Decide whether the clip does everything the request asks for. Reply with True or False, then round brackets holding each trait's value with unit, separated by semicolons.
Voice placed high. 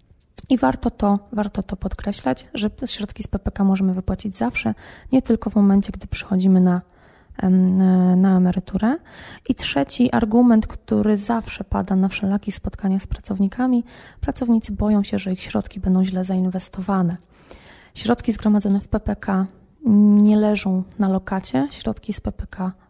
True (200 Hz)